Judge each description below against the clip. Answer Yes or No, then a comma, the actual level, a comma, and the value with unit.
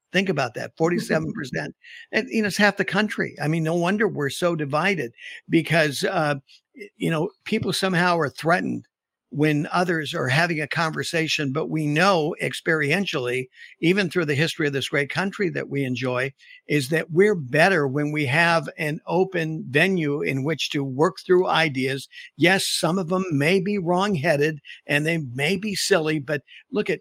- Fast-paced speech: No, average, 175 wpm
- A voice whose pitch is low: No, medium, 165 Hz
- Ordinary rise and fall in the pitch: Yes, average, 4.2 semitones